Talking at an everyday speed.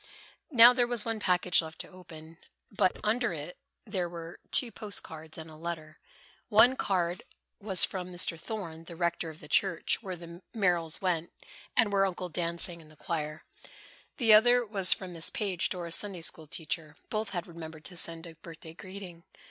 Yes: average, 180 wpm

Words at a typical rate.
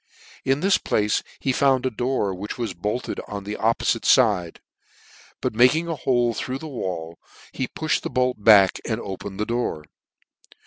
Yes: average, 170 wpm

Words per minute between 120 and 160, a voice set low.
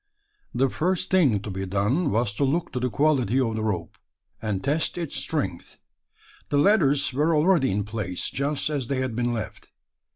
No: average, 185 wpm; low, 130 Hz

